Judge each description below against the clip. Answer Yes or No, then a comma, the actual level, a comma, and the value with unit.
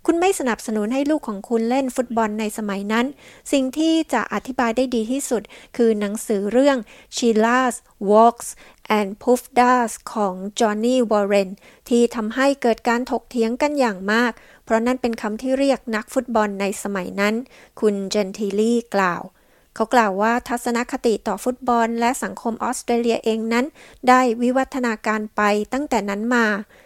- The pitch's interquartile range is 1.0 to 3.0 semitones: Yes, average, 2.7 semitones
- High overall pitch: Yes, high, 235 Hz